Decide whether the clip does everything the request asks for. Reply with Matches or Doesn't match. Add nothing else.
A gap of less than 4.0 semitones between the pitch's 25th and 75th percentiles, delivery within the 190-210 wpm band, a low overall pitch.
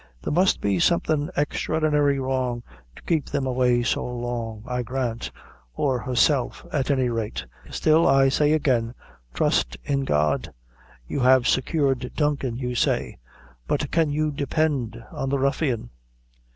Doesn't match